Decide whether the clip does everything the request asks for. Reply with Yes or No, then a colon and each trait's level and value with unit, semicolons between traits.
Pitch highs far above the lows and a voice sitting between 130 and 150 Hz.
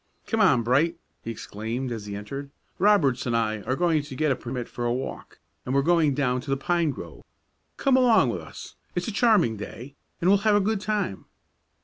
Yes: wide, 6.8 semitones; medium, 140 Hz